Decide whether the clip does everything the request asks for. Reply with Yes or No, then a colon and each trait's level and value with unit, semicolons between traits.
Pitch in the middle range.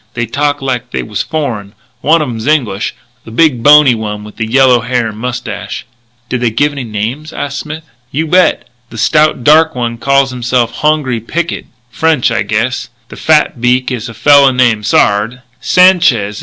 No: low, 125 Hz